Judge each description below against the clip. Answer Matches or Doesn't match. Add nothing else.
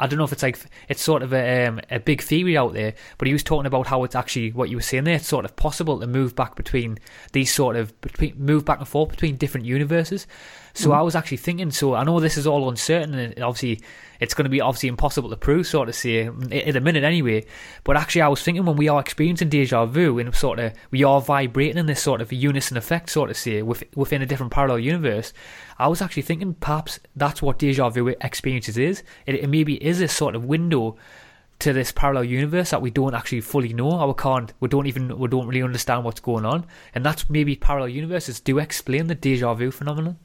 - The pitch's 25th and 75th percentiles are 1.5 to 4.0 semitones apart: Matches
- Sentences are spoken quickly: Matches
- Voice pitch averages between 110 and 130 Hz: Doesn't match